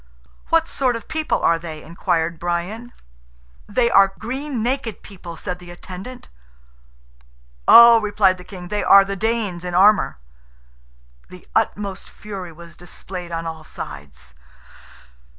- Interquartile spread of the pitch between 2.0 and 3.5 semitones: No, average, 4.4 semitones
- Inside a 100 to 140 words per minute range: Yes, slow, 135 wpm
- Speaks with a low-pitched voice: No, high, 190 Hz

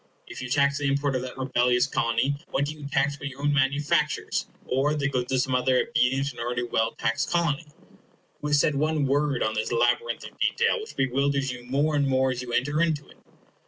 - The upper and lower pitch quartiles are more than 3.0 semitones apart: No, narrow, 2.5 semitones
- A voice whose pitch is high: No, medium, 140 Hz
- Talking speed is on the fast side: Yes, fast, 220 wpm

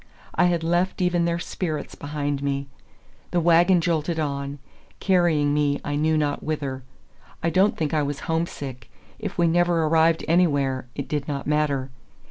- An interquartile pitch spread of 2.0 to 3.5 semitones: Yes, average, 3.1 semitones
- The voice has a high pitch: No, medium, 155 Hz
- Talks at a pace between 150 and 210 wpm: Yes, average, 160 wpm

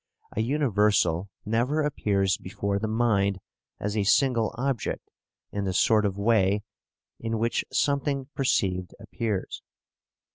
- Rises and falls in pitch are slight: No, average, 3.4 semitones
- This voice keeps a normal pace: No, slow, 120 wpm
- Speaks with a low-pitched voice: Yes, low, 110 Hz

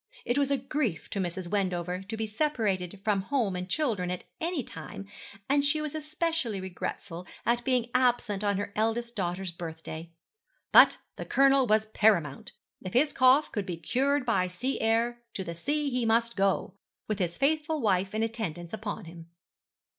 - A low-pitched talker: No, high, 215 Hz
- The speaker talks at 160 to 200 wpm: Yes, average, 175 wpm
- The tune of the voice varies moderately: No, wide, 5.9 semitones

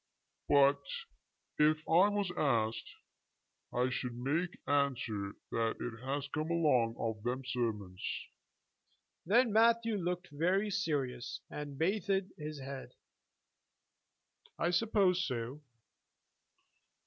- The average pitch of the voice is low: No, medium, 145 Hz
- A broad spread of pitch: Yes, wide, 6.5 semitones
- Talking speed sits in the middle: No, slow, 100 wpm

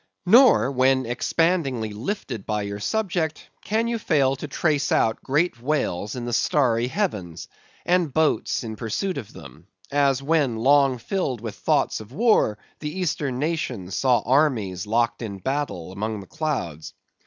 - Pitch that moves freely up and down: Yes, wide, 6.1 semitones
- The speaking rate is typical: Yes, average, 155 wpm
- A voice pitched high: No, low, 130 Hz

